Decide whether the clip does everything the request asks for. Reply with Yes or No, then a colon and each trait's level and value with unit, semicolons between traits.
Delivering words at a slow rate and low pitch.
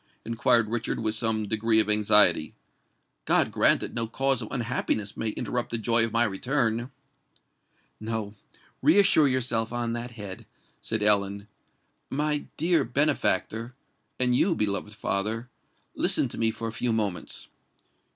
Yes: slow, 130 wpm; low, 115 Hz